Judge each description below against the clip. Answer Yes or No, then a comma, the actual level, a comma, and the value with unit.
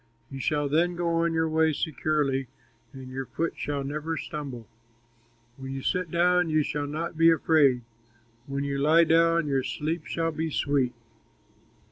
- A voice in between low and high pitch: Yes, medium, 155 Hz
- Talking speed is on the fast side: No, average, 160 wpm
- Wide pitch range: No, average, 2.9 semitones